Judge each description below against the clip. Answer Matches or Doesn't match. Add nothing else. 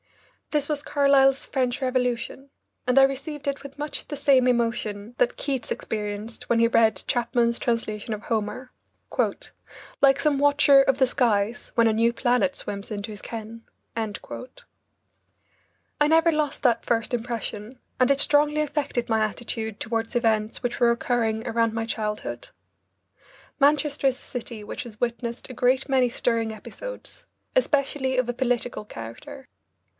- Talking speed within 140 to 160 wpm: Matches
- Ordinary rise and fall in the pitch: Matches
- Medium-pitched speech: Doesn't match